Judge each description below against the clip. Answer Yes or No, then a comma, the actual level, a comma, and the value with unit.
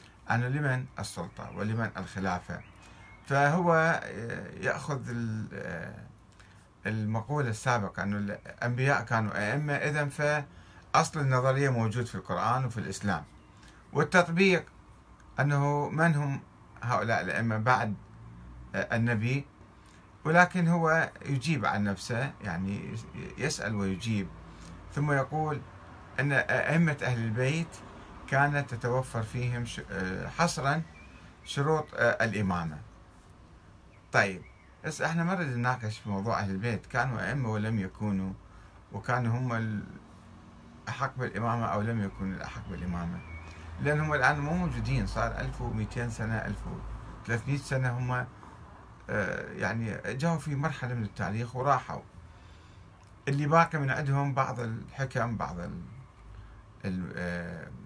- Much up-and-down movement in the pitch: Yes, wide, 5.7 semitones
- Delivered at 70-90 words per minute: No, average, 105 wpm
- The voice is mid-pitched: No, low, 115 Hz